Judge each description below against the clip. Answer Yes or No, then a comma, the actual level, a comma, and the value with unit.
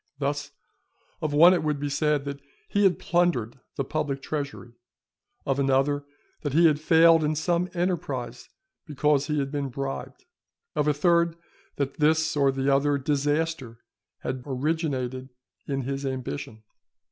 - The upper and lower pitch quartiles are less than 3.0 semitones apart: Yes, narrow, 2.5 semitones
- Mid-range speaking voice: Yes, medium, 145 Hz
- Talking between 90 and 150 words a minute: Yes, average, 145 wpm